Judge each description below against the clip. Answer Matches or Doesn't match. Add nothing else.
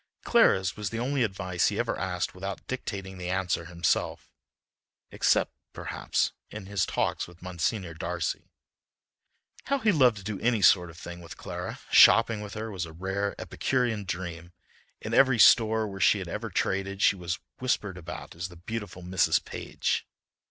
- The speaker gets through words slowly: Doesn't match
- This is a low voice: Matches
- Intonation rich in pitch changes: Doesn't match